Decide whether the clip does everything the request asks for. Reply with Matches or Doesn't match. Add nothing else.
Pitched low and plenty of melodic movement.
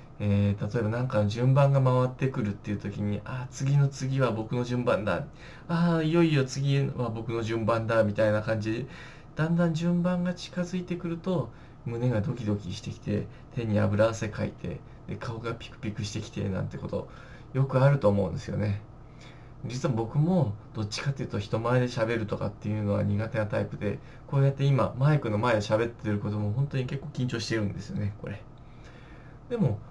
Doesn't match